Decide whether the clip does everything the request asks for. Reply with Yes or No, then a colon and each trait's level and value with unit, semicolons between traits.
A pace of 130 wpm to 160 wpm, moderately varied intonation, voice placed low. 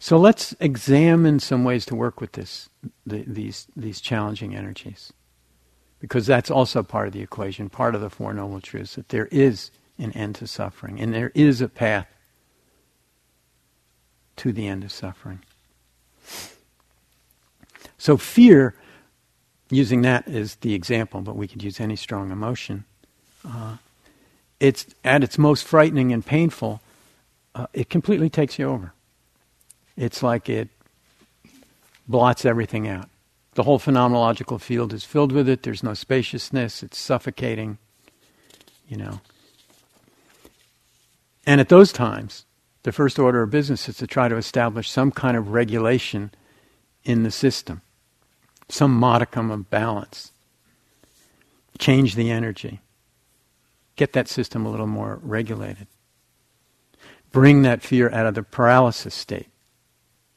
Yes: slow, 135 wpm; average, 4.0 semitones; low, 115 Hz